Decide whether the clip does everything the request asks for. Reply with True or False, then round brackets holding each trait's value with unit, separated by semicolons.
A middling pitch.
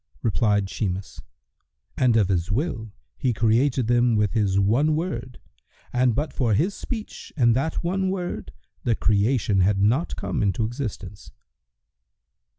False (115 Hz)